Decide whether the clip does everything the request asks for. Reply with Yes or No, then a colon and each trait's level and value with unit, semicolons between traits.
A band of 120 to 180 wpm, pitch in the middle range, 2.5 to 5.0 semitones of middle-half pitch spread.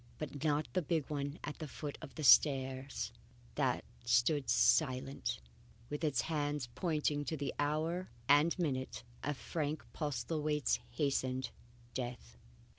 Yes: slow, 135 wpm; medium, 145 Hz; average, 2.8 semitones